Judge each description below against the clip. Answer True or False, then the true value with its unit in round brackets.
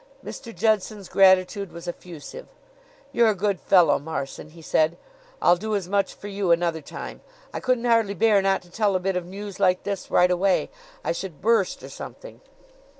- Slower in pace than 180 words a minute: False (185 wpm)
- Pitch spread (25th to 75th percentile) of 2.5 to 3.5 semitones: True (2.9 semitones)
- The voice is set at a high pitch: True (195 Hz)